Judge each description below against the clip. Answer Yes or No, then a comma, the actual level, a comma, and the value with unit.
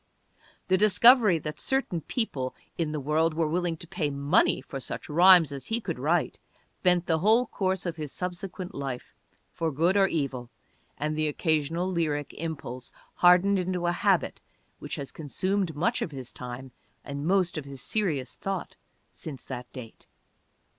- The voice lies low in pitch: No, medium, 165 Hz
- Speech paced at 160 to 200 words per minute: Yes, average, 165 wpm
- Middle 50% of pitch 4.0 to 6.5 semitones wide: Yes, average, 4.5 semitones